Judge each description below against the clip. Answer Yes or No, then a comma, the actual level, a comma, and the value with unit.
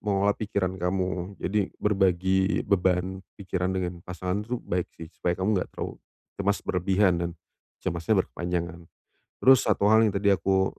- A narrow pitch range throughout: Yes, narrow, 2.0 semitones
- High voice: No, very low, 95 Hz